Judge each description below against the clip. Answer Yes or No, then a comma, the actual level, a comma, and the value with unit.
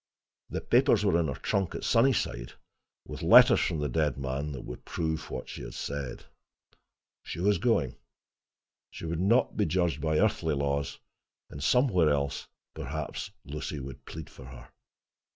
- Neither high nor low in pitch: No, very low, 75 Hz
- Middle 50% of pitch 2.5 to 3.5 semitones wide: No, average, 4.8 semitones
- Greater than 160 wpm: No, average, 155 wpm